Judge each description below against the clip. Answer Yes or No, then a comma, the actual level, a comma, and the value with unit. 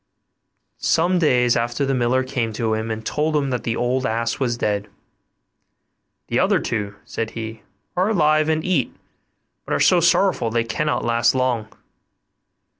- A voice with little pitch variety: No, average, 4.9 semitones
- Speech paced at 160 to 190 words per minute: Yes, average, 165 wpm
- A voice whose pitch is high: No, low, 125 Hz